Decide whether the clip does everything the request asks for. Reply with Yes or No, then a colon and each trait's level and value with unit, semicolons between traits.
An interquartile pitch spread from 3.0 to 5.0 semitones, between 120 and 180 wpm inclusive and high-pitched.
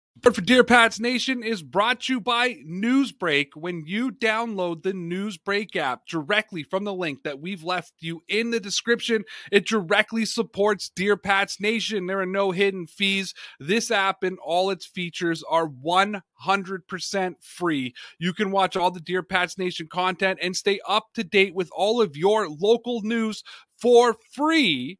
Yes: average, 3.6 semitones; average, 165 wpm; high, 195 Hz